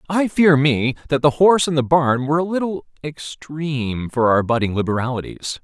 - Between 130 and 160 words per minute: No, average, 180 wpm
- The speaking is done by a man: Yes, male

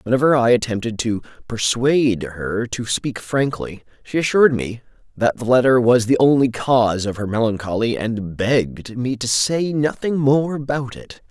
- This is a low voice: Yes, low, 120 Hz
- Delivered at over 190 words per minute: No, average, 165 wpm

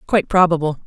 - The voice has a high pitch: No, medium, 170 Hz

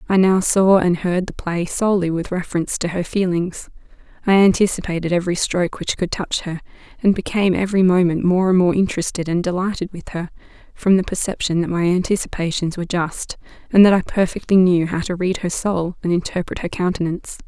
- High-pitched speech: No, medium, 180 Hz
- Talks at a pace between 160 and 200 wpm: Yes, average, 190 wpm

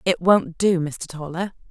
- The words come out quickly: No, average, 175 wpm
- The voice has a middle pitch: Yes, medium, 175 Hz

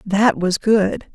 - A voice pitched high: Yes, high, 200 Hz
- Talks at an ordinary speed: Yes, average, 155 wpm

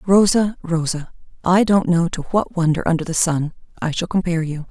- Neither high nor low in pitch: Yes, medium, 175 Hz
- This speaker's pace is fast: No, average, 190 wpm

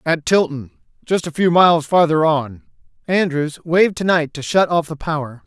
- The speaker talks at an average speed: Yes, average, 175 wpm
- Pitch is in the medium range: Yes, medium, 160 Hz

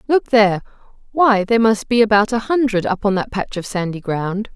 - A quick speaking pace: Yes, fast, 210 wpm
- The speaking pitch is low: No, high, 210 Hz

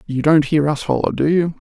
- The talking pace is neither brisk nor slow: No, fast, 250 wpm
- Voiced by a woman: No, male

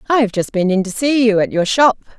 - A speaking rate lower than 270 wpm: No, fast, 275 wpm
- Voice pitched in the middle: No, high, 225 Hz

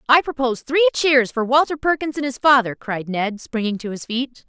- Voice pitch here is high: Yes, very high, 260 Hz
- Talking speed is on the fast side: Yes, fast, 215 wpm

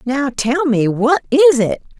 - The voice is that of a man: No, female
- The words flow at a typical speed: Yes, average, 180 wpm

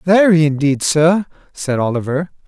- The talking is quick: No, slow, 120 wpm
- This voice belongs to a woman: No, male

